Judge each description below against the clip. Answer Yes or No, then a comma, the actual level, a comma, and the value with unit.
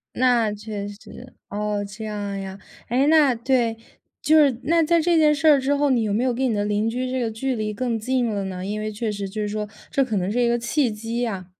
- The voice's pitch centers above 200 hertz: Yes, high, 230 Hz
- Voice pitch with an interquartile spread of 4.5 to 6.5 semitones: No, average, 3.8 semitones